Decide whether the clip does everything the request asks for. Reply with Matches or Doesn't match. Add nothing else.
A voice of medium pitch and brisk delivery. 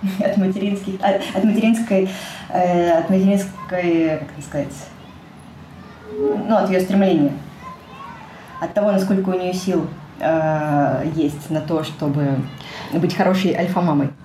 Doesn't match